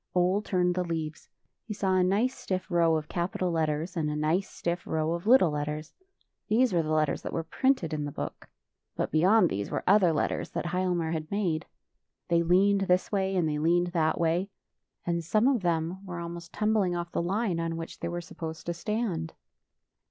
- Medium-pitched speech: Yes, medium, 175 Hz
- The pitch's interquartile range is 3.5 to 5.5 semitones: No, average, 2.8 semitones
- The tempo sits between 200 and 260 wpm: Yes, fast, 205 wpm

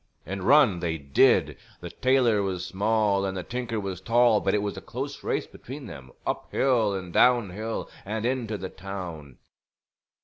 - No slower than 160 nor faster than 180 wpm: Yes, average, 175 wpm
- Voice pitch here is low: Yes, low, 100 Hz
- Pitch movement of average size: Yes, average, 3.7 semitones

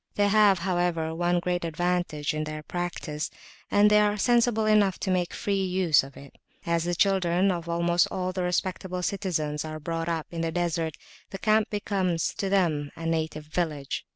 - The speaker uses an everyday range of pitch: Yes, average, 3.0 semitones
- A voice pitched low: No, medium, 175 Hz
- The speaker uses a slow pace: No, average, 180 wpm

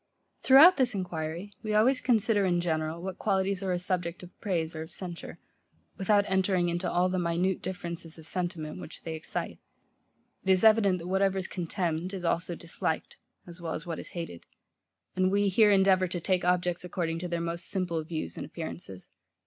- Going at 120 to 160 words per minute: No, average, 190 wpm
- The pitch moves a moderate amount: No, narrow, 2.3 semitones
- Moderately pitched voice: Yes, medium, 180 Hz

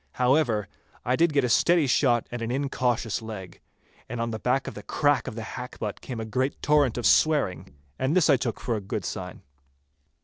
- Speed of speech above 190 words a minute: Yes, fast, 205 wpm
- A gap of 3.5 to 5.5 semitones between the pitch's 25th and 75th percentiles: Yes, average, 3.8 semitones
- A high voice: No, low, 125 Hz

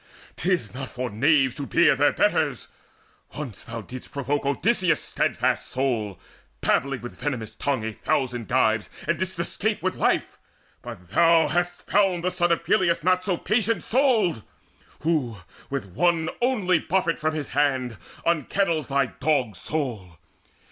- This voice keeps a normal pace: Yes, average, 150 wpm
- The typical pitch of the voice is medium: Yes, medium, 145 Hz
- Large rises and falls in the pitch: Yes, wide, 5.9 semitones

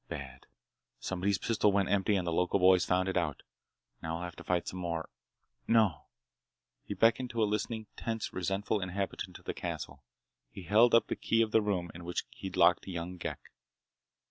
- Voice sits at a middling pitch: No, very low, 95 Hz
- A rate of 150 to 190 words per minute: Yes, average, 185 wpm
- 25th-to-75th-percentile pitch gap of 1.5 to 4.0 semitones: Yes, average, 3.2 semitones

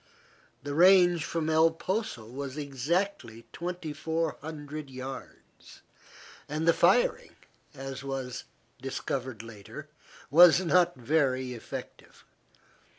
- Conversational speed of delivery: No, slow, 90 wpm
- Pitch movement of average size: Yes, average, 4.2 semitones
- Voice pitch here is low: No, medium, 150 Hz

